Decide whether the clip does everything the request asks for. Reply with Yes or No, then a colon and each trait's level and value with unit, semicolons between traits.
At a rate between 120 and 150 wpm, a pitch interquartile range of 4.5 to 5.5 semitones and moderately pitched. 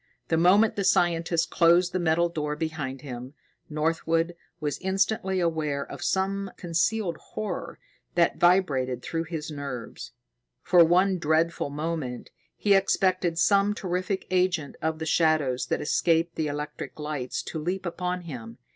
No: average, 140 wpm; average, 3.3 semitones; medium, 165 Hz